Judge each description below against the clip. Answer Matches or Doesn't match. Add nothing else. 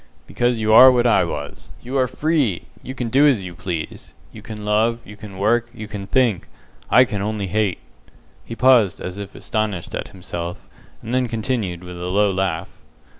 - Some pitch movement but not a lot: Matches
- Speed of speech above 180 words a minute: Matches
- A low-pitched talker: Matches